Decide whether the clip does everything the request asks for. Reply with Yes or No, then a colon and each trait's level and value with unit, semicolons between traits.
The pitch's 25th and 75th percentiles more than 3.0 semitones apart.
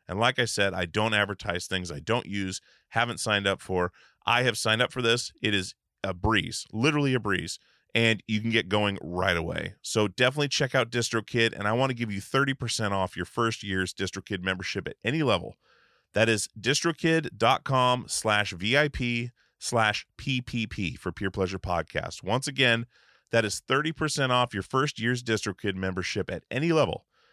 Yes: average, 4.2 semitones